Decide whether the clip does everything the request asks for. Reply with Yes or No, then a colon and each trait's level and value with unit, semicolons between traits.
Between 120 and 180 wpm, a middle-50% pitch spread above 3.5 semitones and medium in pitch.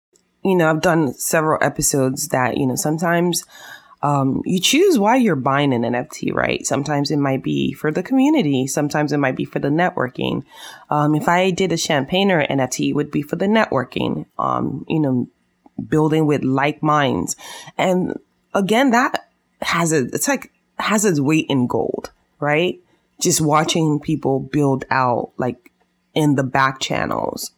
Yes: average, 170 wpm; average, 4.6 semitones; medium, 150 Hz